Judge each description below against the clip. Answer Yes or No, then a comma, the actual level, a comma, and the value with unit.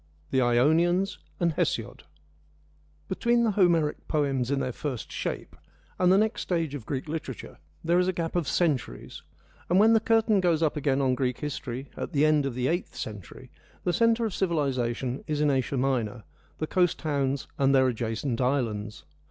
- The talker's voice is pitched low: No, medium, 145 Hz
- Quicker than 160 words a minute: Yes, average, 180 wpm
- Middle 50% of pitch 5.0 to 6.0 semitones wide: Yes, average, 5.3 semitones